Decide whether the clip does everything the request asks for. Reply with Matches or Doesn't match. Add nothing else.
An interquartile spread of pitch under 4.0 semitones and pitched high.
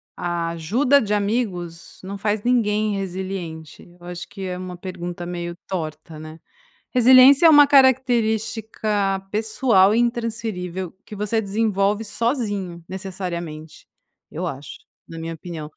Doesn't match